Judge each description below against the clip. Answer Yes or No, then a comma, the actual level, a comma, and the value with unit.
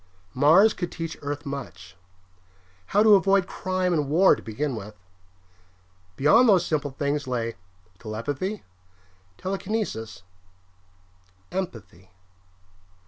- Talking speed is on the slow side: Yes, slow, 100 wpm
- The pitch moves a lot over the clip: Yes, wide, 7.5 semitones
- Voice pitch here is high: No, medium, 150 Hz